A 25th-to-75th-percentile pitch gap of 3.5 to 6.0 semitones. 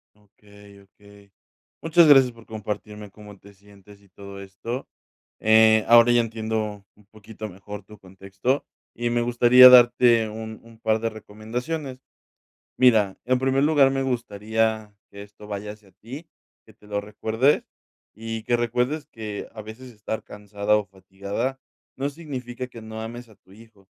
No: average, 2.9 semitones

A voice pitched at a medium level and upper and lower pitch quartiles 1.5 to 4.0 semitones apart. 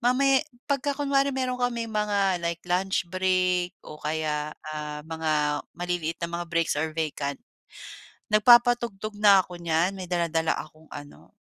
No: medium, 180 Hz; average, 5.2 semitones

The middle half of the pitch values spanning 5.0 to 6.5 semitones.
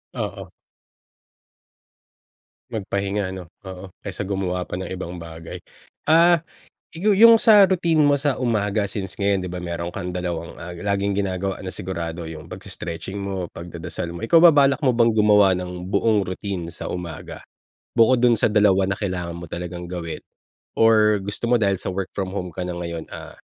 No: average, 3.6 semitones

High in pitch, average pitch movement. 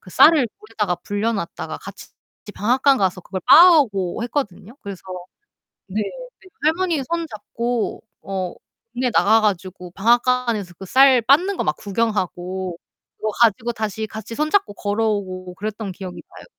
Yes: high, 215 Hz; average, 4.7 semitones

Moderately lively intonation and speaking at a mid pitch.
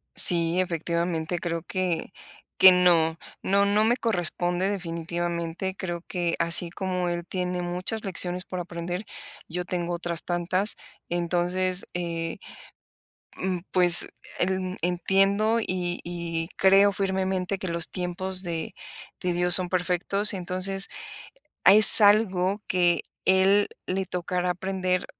No: narrow, 1.6 semitones; medium, 180 Hz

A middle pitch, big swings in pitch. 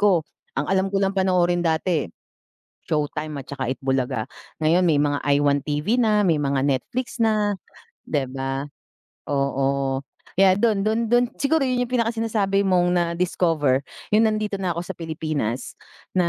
Yes: medium, 170 Hz; wide, 6.3 semitones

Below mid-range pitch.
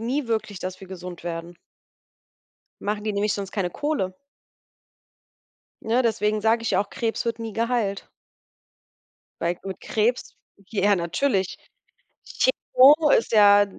No: high, 210 Hz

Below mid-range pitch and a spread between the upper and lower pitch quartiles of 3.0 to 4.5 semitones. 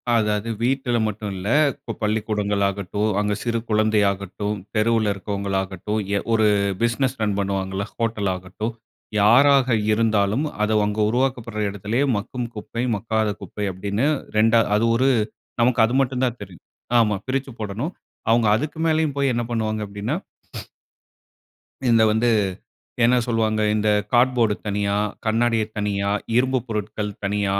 No: low, 110 Hz; narrow, 2.6 semitones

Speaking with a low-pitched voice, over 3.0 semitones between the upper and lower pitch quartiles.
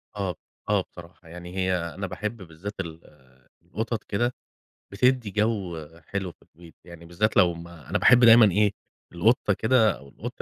Yes: very low, 95 Hz; average, 4.0 semitones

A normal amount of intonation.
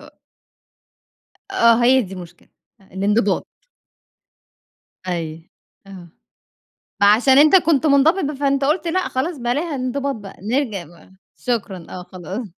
No: wide, 6.5 semitones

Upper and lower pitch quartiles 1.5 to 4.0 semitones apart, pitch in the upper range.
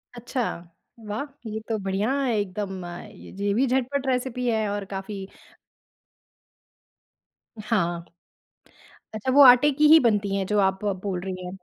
No: average, 4.5 semitones; high, 210 Hz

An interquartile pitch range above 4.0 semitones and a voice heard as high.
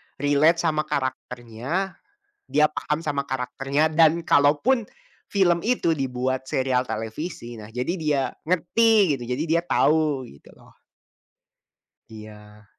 No: average, 4.8 semitones; medium, 145 Hz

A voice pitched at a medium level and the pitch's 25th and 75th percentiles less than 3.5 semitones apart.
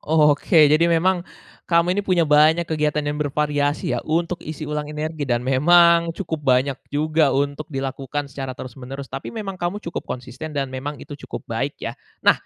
Yes: medium, 150 Hz; average, 3.0 semitones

